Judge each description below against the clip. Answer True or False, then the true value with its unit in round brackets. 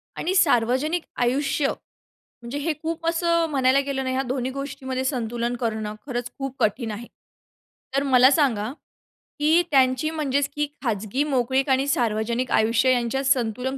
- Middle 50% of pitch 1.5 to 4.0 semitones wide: True (2.9 semitones)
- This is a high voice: True (260 Hz)